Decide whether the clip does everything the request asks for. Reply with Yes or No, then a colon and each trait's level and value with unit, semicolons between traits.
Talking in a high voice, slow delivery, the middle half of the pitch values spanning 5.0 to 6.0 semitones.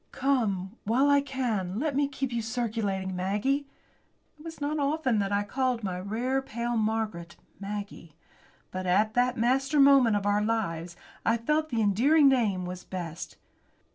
No: high, 225 Hz; average, 165 wpm; average, 5.3 semitones